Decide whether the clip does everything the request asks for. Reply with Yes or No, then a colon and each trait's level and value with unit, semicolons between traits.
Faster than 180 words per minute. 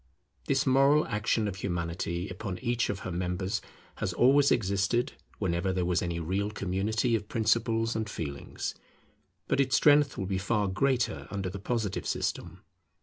No: average, 155 wpm